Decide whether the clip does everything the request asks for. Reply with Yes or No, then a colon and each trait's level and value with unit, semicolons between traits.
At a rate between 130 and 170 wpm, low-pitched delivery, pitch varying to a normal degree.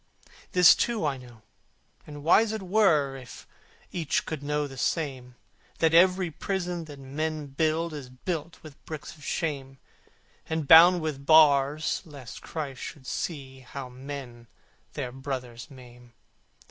No: average, 140 wpm; medium, 145 Hz; average, 3.4 semitones